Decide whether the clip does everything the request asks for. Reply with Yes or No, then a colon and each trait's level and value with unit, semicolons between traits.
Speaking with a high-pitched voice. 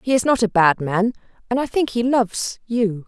Yes: high, 225 Hz